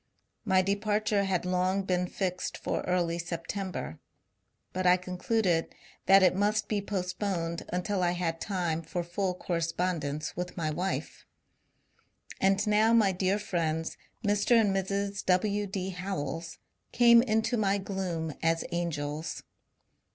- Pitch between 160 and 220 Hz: Yes, medium, 185 Hz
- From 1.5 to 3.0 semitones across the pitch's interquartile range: Yes, average, 2.7 semitones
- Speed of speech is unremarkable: No, slow, 130 wpm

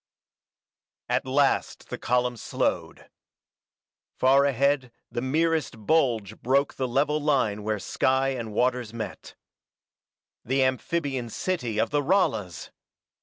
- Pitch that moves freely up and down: No, average, 3.4 semitones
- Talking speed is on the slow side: Yes, slow, 115 wpm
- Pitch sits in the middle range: No, low, 130 Hz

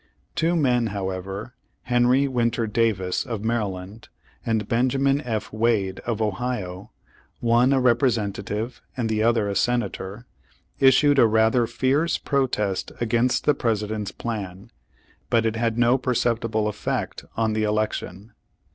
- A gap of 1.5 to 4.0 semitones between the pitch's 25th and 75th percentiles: Yes, average, 2.7 semitones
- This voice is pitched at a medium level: No, low, 115 Hz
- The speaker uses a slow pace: Yes, slow, 130 wpm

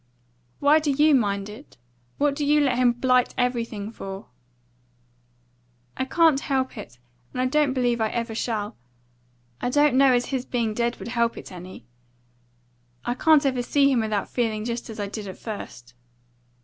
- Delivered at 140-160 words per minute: No, average, 175 wpm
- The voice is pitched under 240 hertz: No, high, 245 Hz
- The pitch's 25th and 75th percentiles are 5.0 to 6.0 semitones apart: No, average, 3.9 semitones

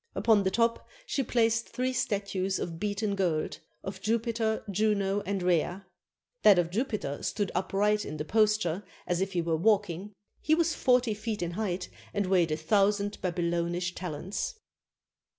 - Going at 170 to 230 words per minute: No, average, 155 wpm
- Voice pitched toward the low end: No, high, 200 Hz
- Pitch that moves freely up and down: No, average, 3.5 semitones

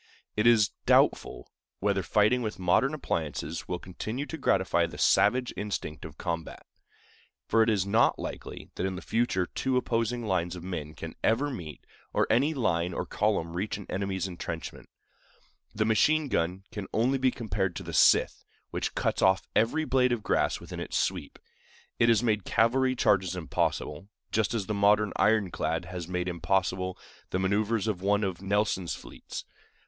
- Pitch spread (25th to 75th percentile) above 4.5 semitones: No, average, 4.1 semitones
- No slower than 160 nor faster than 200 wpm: Yes, average, 170 wpm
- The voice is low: Yes, low, 100 Hz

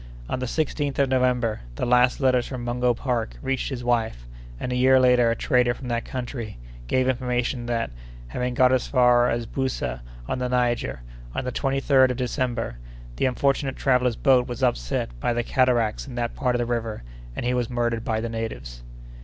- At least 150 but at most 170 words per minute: No, average, 195 wpm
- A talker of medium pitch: No, low, 125 Hz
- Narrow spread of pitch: Yes, narrow, 1.6 semitones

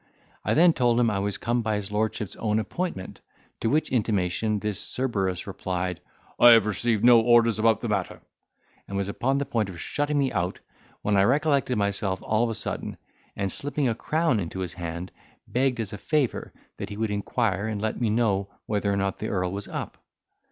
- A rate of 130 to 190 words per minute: No, average, 200 wpm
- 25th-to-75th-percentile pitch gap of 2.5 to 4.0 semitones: Yes, average, 3.5 semitones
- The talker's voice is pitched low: Yes, low, 110 Hz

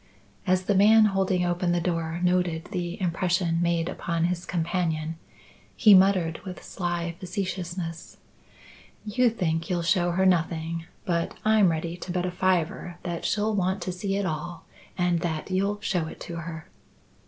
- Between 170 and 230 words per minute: No, average, 160 wpm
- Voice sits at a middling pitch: Yes, medium, 175 Hz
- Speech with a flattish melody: Yes, narrow, 2.0 semitones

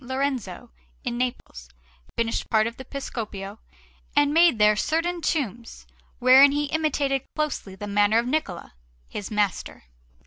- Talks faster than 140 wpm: No, slow, 135 wpm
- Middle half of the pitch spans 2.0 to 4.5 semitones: No, average, 5.3 semitones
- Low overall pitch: No, high, 245 Hz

